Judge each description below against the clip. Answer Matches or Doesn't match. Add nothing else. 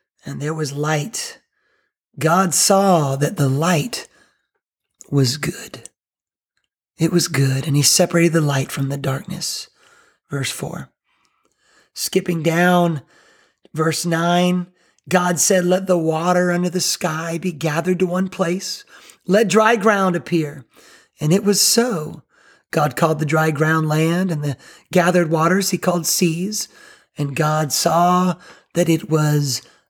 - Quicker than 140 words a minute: Doesn't match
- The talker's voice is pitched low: Doesn't match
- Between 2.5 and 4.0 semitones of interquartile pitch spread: Matches